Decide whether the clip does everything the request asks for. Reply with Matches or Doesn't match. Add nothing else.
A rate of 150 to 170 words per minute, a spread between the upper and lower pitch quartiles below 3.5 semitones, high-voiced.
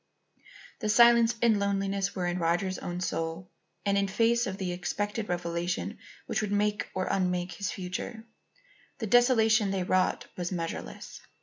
Matches